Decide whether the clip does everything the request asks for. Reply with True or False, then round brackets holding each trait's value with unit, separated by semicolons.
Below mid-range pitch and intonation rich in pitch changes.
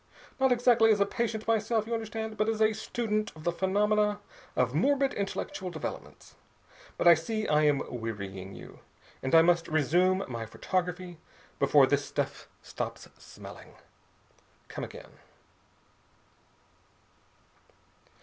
False (200 Hz; 5.7 semitones)